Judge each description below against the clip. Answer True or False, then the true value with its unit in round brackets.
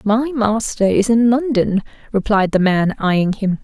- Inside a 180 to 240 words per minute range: False (165 wpm)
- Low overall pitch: False (215 Hz)